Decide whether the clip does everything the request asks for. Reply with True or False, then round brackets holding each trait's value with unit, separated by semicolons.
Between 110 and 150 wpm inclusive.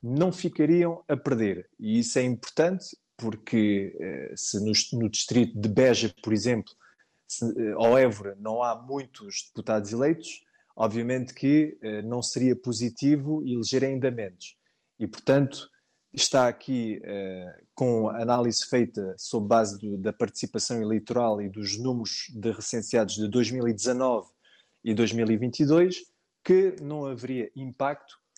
True (135 wpm)